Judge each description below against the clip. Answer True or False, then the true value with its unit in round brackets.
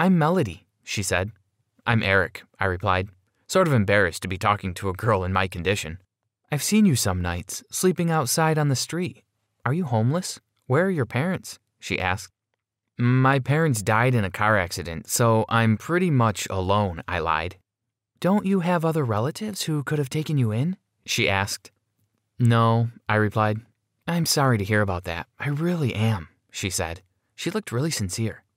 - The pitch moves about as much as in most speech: False (6.9 semitones)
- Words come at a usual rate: True (175 wpm)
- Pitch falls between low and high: False (115 Hz)